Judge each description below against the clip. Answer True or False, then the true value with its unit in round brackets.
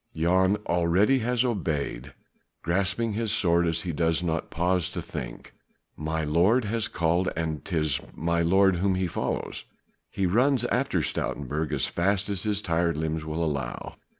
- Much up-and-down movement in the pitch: False (3.7 semitones)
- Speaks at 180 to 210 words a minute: False (150 wpm)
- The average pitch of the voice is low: True (85 Hz)